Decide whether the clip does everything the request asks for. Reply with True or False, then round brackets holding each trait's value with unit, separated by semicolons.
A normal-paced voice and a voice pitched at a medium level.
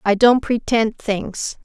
False (145 wpm; 220 Hz)